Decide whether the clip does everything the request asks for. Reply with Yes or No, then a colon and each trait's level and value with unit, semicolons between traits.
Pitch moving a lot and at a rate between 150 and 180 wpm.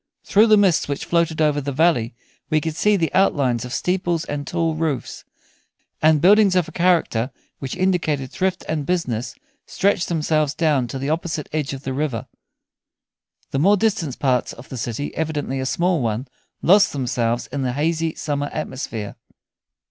No: average, 4.5 semitones; average, 170 wpm